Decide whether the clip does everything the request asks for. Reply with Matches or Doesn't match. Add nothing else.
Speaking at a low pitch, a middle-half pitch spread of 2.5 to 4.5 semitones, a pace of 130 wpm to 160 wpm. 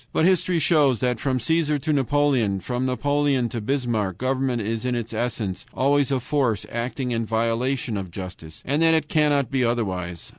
Doesn't match